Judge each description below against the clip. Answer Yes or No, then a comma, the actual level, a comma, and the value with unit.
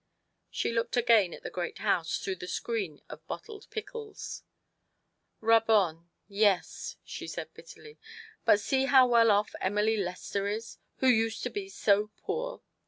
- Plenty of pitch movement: No, average, 4.4 semitones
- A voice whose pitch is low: No, high, 220 Hz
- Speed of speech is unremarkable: Yes, average, 165 wpm